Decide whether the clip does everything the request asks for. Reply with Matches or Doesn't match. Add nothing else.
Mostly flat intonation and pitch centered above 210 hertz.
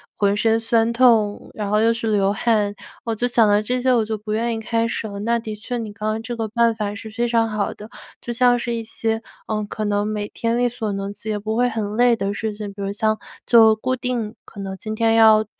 Matches